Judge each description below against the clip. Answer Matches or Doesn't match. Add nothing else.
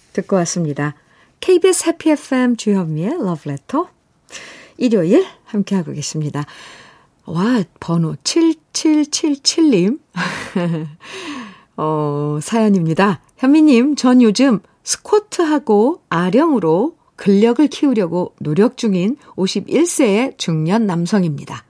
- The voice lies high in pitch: Matches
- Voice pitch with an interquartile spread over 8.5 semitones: Matches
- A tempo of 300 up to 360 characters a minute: Doesn't match